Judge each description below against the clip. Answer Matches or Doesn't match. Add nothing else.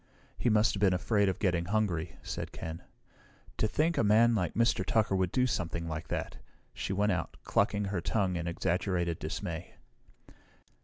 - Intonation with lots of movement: Doesn't match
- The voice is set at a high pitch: Doesn't match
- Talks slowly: Doesn't match